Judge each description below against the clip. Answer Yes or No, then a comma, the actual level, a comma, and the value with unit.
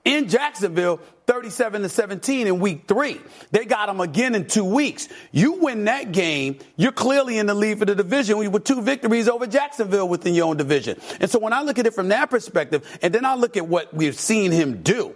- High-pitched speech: Yes, high, 215 Hz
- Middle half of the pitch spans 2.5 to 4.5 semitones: No, average, 5.3 semitones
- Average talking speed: No, fast, 220 wpm